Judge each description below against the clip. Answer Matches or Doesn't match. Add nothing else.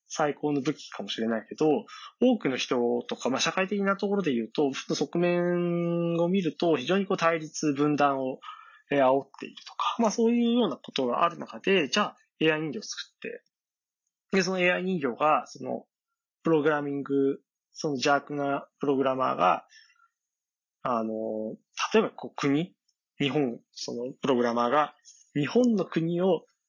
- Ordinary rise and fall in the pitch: Doesn't match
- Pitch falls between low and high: Matches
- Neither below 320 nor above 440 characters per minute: Doesn't match